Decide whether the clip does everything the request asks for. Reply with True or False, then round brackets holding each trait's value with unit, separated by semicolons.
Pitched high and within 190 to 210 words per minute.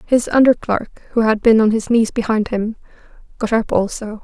True (220 Hz; 200 wpm)